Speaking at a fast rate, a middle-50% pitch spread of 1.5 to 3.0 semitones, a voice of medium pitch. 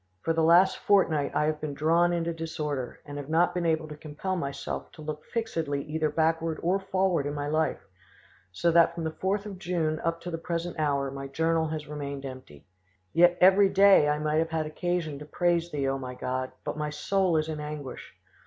Yes: fast, 210 wpm; average, 2.7 semitones; medium, 160 Hz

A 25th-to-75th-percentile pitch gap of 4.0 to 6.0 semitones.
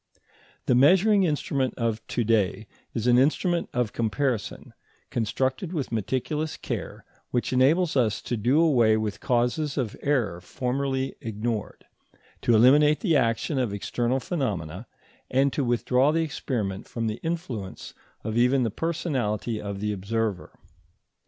Yes: average, 4.3 semitones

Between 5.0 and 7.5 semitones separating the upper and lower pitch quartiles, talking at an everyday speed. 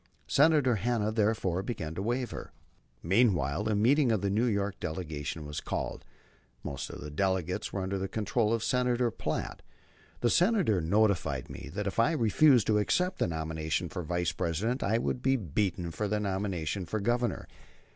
Yes: average, 5.3 semitones; average, 170 wpm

